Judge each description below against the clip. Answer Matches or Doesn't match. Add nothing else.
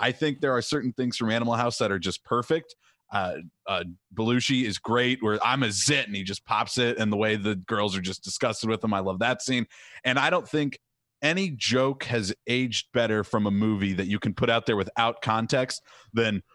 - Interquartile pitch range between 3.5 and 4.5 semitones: Doesn't match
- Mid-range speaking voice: Doesn't match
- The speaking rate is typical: Doesn't match